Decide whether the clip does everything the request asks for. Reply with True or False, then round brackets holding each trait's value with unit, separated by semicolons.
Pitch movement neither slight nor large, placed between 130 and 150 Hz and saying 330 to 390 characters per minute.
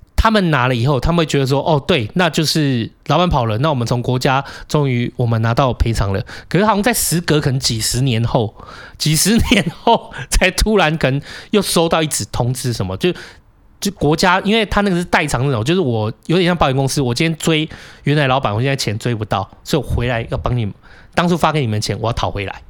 False (6.1 semitones; 140 Hz; 335 characters per minute)